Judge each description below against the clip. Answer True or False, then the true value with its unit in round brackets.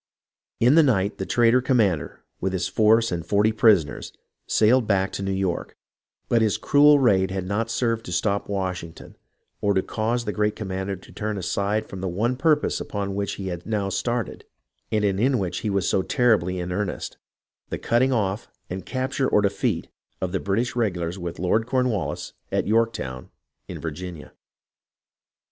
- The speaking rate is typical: True (175 wpm)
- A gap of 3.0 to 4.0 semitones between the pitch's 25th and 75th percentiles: True (3.5 semitones)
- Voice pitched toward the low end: True (100 Hz)